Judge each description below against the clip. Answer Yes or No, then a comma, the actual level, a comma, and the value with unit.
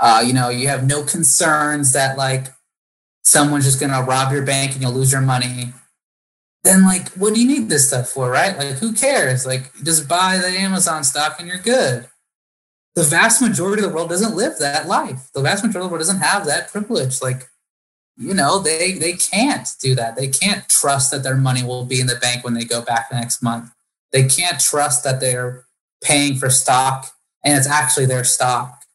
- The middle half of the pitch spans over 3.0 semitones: Yes, average, 5.1 semitones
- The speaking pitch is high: No, medium, 140 Hz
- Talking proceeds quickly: Yes, fast, 210 wpm